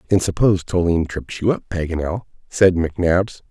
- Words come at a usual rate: Yes, average, 155 wpm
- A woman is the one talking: No, male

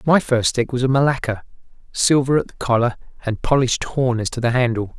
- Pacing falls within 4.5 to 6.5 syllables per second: Yes, 5.8 syllables/s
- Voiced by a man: Yes, male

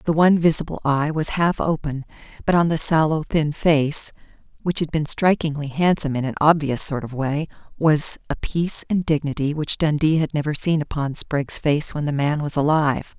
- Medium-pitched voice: Yes, medium, 150 Hz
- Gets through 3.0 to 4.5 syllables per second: No, 5.2 syllables/s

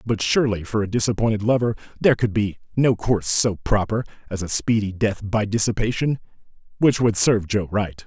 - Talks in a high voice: No, low, 105 Hz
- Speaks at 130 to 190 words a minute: Yes, average, 170 wpm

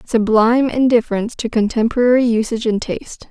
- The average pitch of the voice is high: Yes, high, 230 Hz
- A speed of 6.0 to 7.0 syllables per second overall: Yes, 6.3 syllables/s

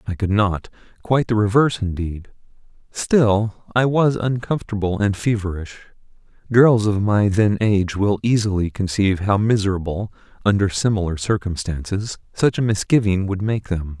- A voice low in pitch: Yes, low, 105 Hz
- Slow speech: Yes, slow, 130 wpm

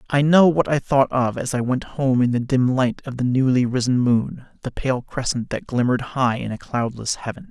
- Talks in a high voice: No, low, 130 Hz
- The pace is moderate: No, fast, 230 wpm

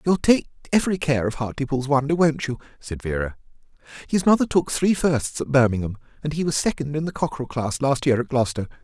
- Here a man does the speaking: Yes, male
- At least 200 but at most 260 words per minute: Yes, fast, 205 wpm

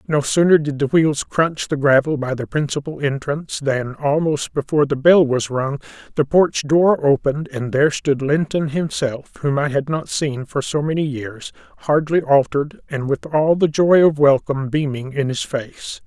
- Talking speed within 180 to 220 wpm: Yes, average, 185 wpm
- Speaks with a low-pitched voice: No, medium, 145 Hz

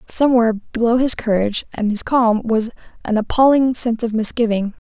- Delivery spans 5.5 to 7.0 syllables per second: Yes, 5.7 syllables/s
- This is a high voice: Yes, high, 230 Hz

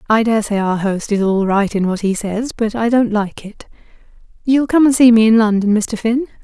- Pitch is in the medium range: No, high, 220 Hz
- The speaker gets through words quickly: Yes, fast, 240 wpm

